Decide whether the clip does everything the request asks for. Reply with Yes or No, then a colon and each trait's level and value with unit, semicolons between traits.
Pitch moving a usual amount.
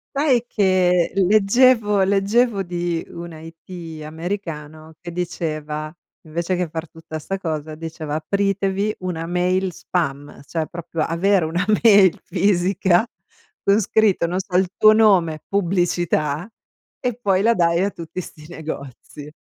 Yes: average, 3.5 semitones